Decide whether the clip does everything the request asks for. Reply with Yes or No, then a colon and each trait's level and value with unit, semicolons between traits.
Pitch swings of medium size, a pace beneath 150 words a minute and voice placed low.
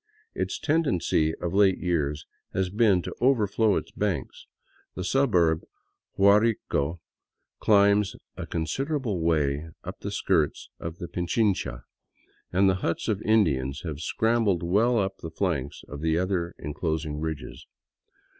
Yes: average, 4.5 semitones; slow, 135 wpm; very low, 90 Hz